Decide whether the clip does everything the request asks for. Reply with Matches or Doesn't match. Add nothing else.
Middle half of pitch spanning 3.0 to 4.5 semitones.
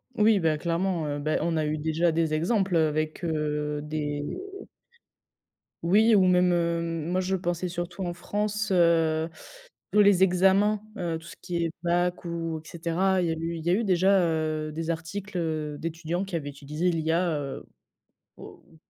Doesn't match